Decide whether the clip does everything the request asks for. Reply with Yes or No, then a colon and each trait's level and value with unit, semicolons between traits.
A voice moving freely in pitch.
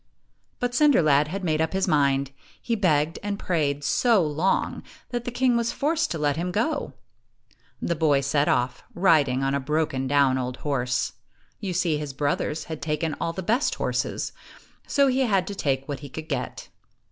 Yes: wide, 5.8 semitones